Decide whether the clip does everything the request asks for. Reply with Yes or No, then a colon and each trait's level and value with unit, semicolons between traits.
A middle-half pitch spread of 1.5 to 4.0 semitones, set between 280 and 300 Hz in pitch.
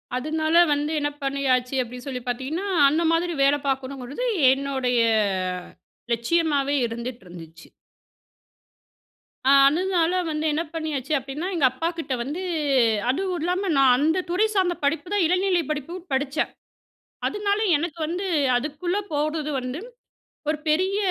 No: average, 4.4 semitones; very high, 295 Hz